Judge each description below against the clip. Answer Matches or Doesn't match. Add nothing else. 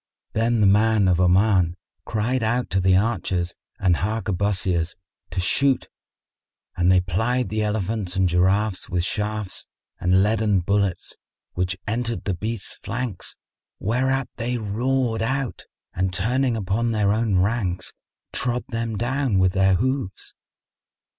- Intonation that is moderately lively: Matches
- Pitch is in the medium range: Doesn't match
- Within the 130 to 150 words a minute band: Matches